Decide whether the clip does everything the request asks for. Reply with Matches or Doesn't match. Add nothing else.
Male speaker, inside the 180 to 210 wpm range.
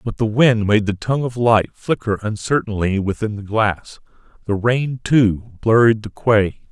Doesn't match